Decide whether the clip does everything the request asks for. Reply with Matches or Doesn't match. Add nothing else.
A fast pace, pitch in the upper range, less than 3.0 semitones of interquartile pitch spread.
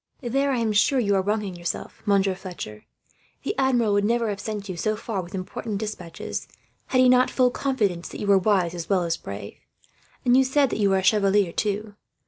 Doesn't match